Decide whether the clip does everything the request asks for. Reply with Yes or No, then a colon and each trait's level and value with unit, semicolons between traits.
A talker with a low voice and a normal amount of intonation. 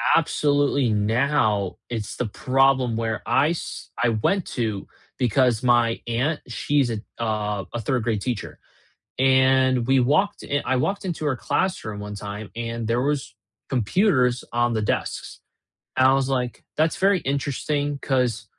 Yes: low, 125 Hz; average, 3.7 semitones